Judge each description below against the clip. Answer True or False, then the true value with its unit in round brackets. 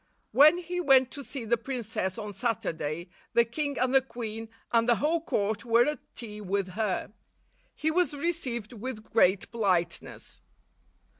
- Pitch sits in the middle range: False (235 Hz)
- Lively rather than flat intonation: False (4.6 semitones)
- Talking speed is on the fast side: False (155 wpm)